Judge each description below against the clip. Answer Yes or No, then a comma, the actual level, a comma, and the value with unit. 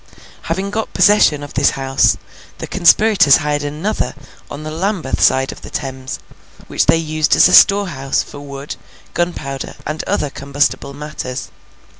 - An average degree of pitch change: Yes, average, 3.9 semitones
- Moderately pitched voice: Yes, medium, 150 Hz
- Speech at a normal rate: Yes, average, 150 wpm